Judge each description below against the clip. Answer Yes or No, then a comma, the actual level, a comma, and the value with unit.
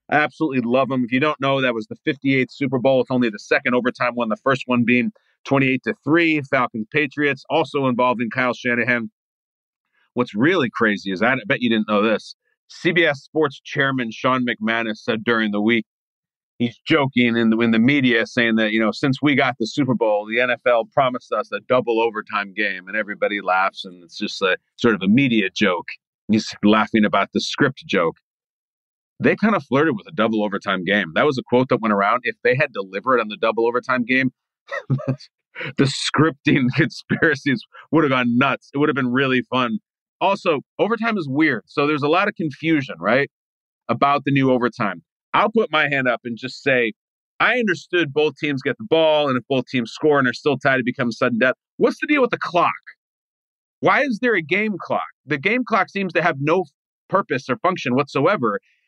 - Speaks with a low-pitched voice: Yes, low, 130 Hz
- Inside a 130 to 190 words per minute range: No, fast, 205 wpm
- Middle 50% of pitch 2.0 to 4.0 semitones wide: No, average, 4.5 semitones